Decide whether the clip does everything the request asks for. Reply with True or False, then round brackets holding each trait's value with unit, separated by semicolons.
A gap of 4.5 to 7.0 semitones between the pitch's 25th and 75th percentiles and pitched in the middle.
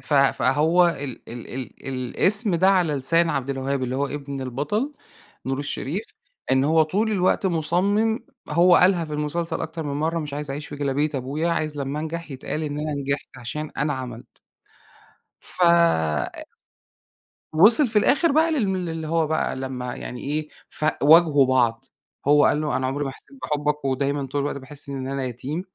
False (3.8 semitones; 150 Hz)